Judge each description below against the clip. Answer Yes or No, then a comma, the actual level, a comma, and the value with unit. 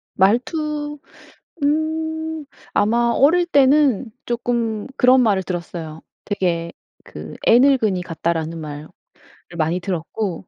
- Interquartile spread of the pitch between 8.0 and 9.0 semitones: Yes, wide, 8.6 semitones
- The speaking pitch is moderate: No, high, 225 Hz